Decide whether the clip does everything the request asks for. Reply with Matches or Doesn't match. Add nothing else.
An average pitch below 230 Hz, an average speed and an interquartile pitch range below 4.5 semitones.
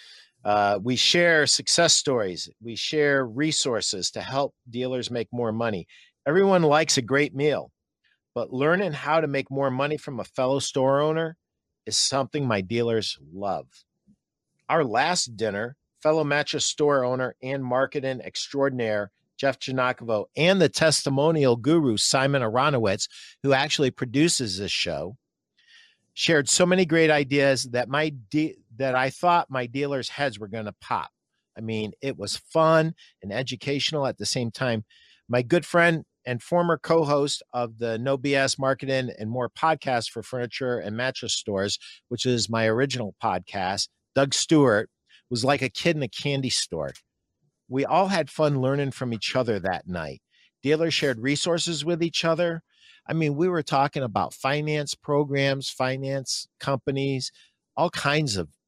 Matches